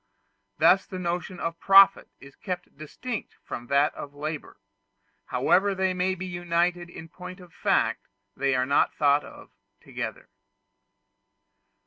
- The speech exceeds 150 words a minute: No, slow, 135 wpm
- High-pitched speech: No, medium, 175 Hz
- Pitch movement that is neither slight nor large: Yes, average, 3.9 semitones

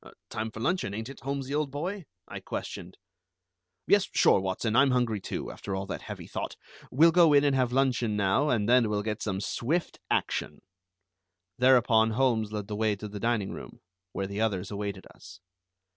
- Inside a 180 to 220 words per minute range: Yes, average, 185 wpm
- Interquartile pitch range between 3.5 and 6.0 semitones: Yes, average, 4.7 semitones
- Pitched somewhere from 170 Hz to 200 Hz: No, low, 110 Hz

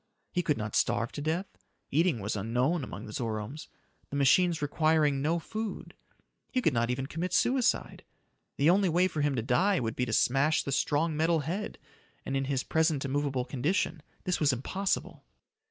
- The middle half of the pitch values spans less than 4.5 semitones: No, average, 4.8 semitones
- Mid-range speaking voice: Yes, medium, 145 Hz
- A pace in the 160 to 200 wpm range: Yes, average, 180 wpm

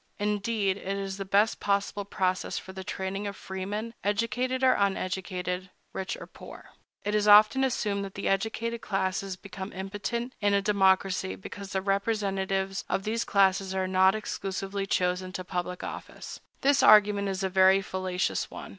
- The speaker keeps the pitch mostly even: Yes, narrow, 1.5 semitones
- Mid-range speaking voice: No, high, 195 Hz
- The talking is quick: No, average, 160 wpm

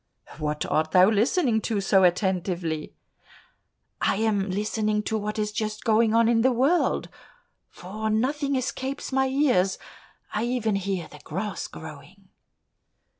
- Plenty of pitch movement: No, average, 3.8 semitones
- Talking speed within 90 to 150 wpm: Yes, slow, 135 wpm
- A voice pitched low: No, high, 215 Hz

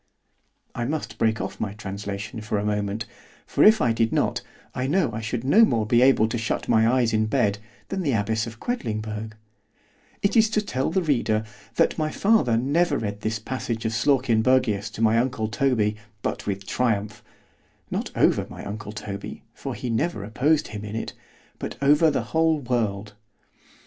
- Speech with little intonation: No, average, 4.0 semitones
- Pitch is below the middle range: Yes, low, 115 Hz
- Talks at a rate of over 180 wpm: No, average, 175 wpm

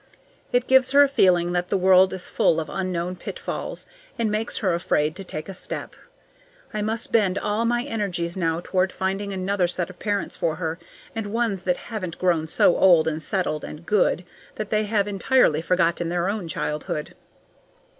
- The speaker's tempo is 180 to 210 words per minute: Yes, average, 185 wpm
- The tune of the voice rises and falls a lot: No, average, 3.4 semitones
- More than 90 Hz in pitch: Yes, medium, 185 Hz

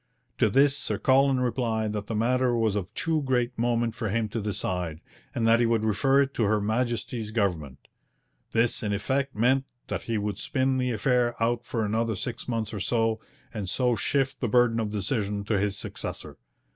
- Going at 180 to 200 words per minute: Yes, average, 195 wpm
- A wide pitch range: No, average, 3.0 semitones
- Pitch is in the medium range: No, low, 115 Hz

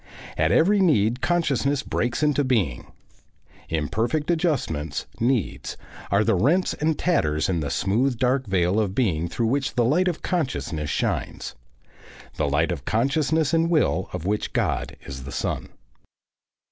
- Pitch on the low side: Yes, low, 120 Hz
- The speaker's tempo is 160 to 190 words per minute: No, average, 145 wpm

